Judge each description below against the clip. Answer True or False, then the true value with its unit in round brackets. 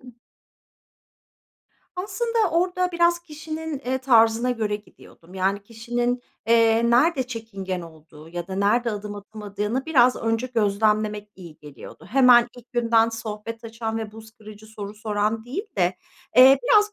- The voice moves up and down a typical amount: True (3.4 semitones)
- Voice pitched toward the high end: True (225 Hz)